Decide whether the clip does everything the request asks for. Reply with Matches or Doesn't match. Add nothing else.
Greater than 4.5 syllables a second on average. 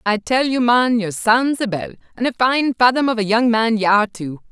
Matches